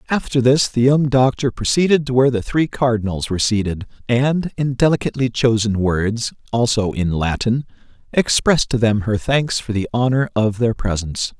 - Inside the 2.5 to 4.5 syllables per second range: No, 5.2 syllables/s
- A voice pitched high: No, low, 120 Hz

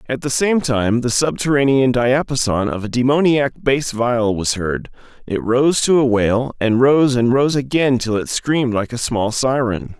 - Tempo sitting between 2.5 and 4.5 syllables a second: Yes, 4.4 syllables/s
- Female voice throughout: No, male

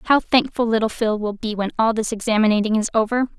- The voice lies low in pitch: No, high, 220 Hz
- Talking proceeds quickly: Yes, fast, 215 wpm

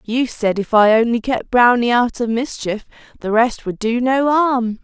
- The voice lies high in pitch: Yes, high, 235 Hz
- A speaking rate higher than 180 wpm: Yes, average, 200 wpm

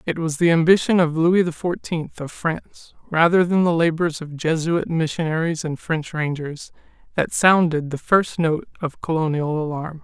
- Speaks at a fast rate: No, average, 165 wpm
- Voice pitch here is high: No, medium, 160 Hz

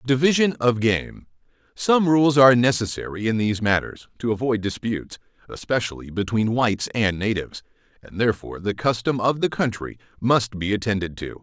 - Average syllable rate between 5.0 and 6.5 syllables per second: Yes, 5.6 syllables/s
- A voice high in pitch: No, low, 115 Hz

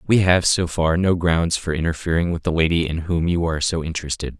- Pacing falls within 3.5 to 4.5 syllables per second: No, 5.9 syllables/s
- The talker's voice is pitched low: Yes, very low, 85 Hz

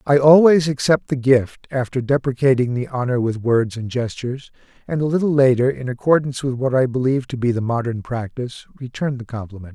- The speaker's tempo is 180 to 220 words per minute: Yes, average, 190 wpm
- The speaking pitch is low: Yes, low, 130 Hz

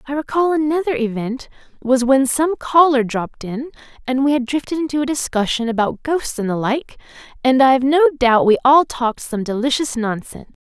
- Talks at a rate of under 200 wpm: Yes, average, 175 wpm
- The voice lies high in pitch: Yes, very high, 265 Hz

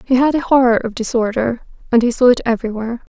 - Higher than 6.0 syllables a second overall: Yes, 6.7 syllables/s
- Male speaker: No, female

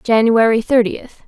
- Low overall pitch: No, high, 225 Hz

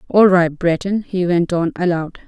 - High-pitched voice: No, medium, 180 Hz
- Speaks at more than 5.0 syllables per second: No, 4.5 syllables/s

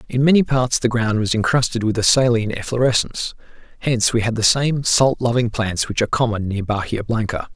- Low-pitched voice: Yes, low, 115 Hz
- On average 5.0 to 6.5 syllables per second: Yes, 5.8 syllables/s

